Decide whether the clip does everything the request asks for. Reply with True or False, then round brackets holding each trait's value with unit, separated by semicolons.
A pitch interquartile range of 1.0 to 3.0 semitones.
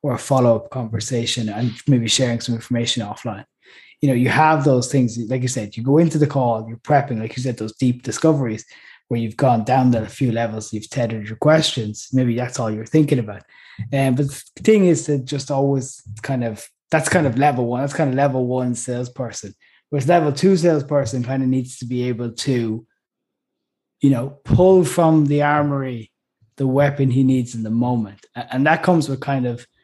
False (3.5 semitones)